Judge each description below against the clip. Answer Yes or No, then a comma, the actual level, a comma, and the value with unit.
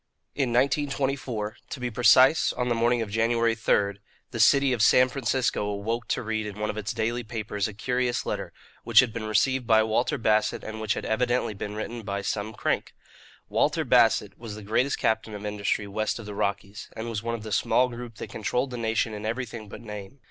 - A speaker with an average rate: No, fast, 215 wpm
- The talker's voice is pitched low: Yes, low, 110 Hz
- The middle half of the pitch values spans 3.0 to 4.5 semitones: No, narrow, 2.5 semitones